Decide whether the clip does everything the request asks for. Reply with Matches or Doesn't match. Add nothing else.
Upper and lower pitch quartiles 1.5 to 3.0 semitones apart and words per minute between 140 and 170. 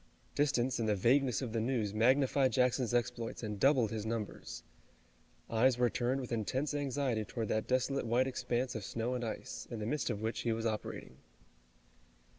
Doesn't match